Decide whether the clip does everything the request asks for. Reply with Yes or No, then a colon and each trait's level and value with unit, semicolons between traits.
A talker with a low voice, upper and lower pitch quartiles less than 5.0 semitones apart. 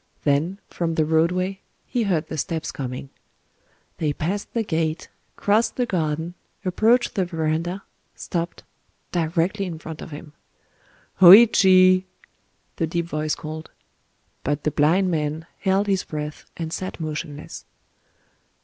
No: medium, 165 Hz; average, 3.3 semitones